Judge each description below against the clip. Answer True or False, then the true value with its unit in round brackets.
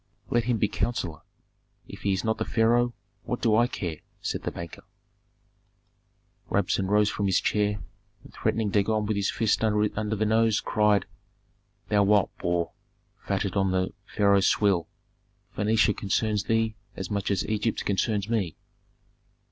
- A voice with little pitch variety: True (1.9 semitones)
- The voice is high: False (105 Hz)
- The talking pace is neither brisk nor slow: True (150 wpm)